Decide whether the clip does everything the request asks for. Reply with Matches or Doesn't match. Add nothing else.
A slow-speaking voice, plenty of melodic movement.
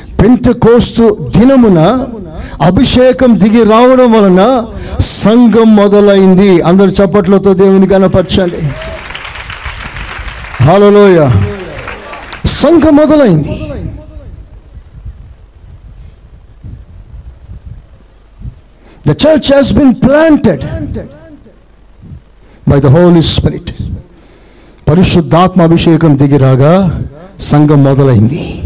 Matches